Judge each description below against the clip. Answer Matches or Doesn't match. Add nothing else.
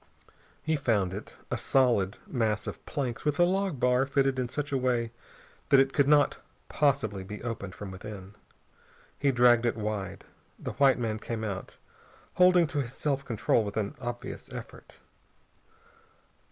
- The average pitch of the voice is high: Doesn't match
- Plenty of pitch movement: Doesn't match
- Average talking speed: Matches